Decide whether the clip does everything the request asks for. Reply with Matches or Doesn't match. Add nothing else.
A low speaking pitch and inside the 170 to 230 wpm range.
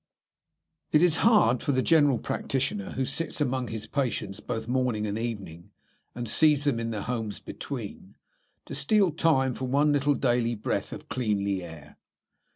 Doesn't match